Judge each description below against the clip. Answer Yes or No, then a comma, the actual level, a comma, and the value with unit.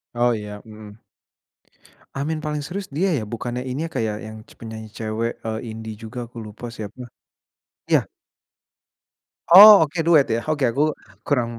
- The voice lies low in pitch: Yes, low, 120 Hz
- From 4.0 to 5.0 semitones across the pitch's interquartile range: Yes, average, 4.6 semitones